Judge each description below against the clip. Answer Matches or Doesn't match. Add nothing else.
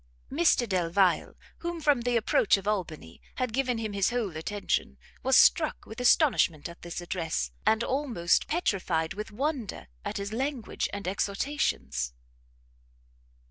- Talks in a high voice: Matches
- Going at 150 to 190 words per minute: Doesn't match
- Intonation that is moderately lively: Doesn't match